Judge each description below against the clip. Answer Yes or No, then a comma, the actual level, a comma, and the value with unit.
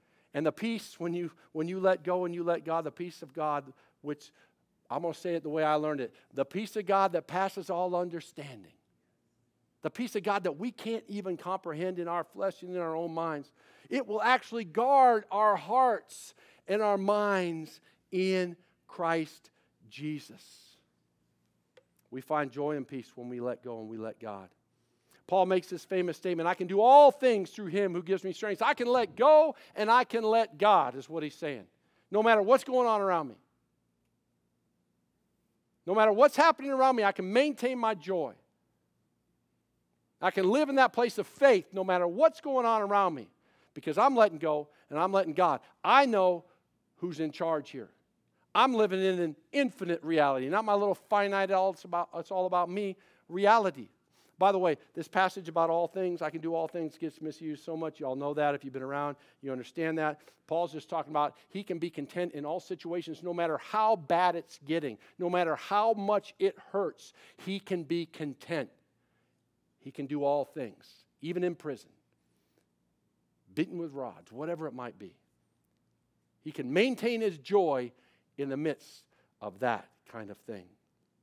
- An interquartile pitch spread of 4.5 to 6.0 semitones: Yes, average, 5.2 semitones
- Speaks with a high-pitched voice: No, medium, 175 Hz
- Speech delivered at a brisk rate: No, average, 190 wpm